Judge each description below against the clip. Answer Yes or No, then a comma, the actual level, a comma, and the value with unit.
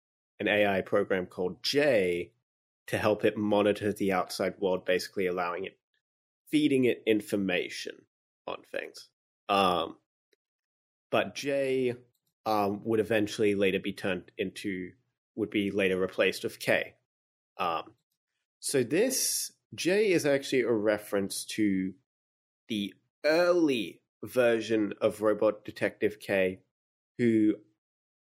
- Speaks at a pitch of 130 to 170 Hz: No, low, 105 Hz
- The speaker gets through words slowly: Yes, slow, 110 wpm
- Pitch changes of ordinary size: Yes, average, 3.1 semitones